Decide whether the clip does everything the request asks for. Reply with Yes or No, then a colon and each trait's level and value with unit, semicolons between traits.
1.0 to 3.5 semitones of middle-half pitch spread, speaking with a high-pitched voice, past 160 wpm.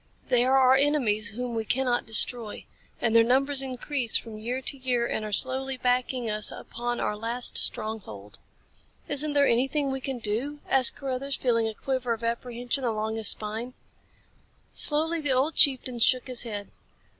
Yes: average, 2.9 semitones; high, 245 Hz; average, 170 wpm